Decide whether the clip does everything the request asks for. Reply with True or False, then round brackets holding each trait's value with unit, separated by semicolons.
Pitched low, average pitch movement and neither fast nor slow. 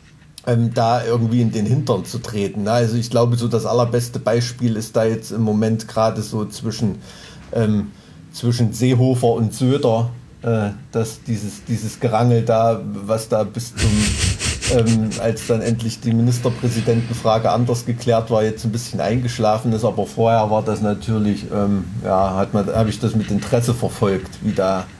False (115 Hz; 1.8 semitones; 160 wpm)